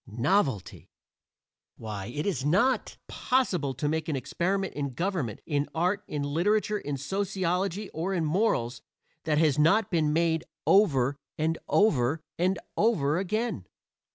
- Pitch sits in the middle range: Yes, medium, 165 Hz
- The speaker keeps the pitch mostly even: No, wide, 5.5 semitones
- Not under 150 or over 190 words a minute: No, slow, 135 wpm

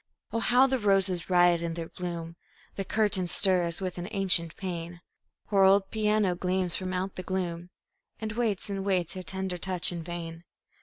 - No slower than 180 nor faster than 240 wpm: Yes, average, 185 wpm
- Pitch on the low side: No, medium, 185 Hz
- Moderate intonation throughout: No, narrow, 2.1 semitones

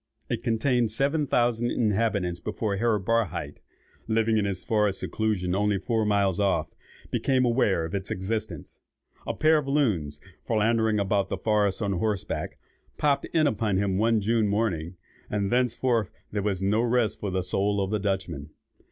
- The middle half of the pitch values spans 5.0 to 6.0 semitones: No, average, 3.0 semitones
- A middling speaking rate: Yes, average, 160 wpm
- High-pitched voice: No, low, 105 Hz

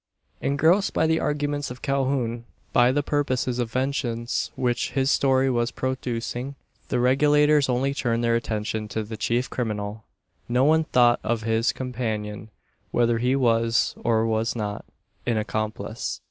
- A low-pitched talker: Yes, low, 120 Hz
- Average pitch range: Yes, average, 3.0 semitones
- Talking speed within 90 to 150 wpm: Yes, average, 145 wpm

